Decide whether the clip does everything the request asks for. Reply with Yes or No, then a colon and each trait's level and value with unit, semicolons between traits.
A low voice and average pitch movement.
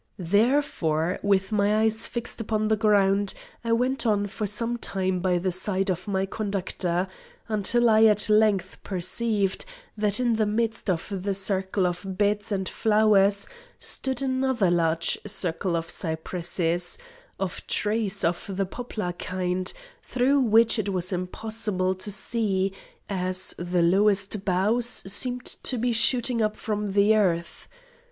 No: high, 200 Hz; average, 3.0 semitones